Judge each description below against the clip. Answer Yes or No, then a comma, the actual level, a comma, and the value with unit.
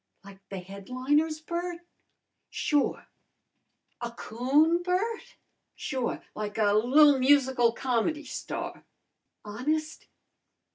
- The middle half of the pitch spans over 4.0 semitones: Yes, average, 5.3 semitones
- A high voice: Yes, very high, 265 Hz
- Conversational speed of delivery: No, slow, 90 wpm